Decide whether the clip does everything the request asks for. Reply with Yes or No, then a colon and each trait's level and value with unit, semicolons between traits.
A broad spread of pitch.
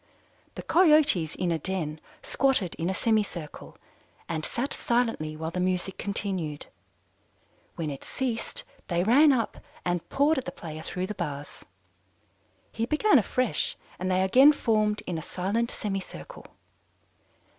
Yes: wide, 6.1 semitones